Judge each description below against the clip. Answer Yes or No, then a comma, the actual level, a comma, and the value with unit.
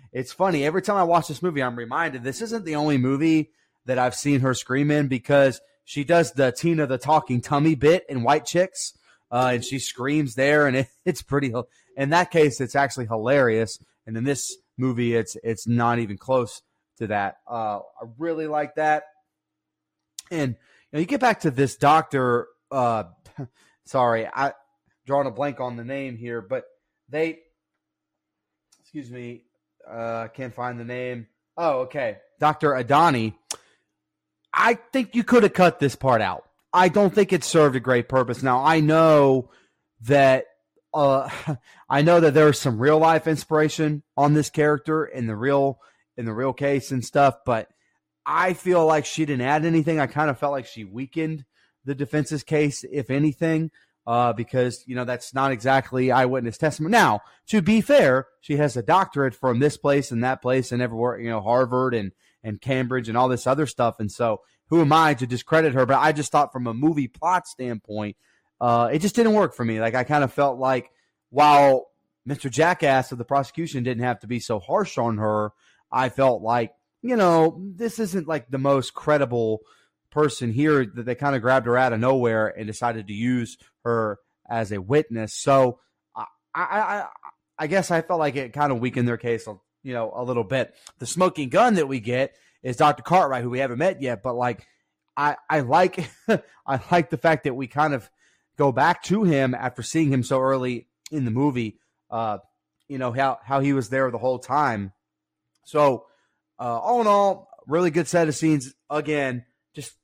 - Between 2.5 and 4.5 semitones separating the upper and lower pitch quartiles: Yes, average, 4.0 semitones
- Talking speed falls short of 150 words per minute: No, average, 190 wpm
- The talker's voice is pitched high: No, low, 135 Hz